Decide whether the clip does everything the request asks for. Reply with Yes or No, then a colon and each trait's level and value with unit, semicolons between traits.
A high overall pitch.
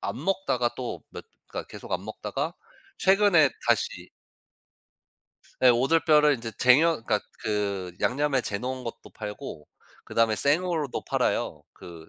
No: low, 130 Hz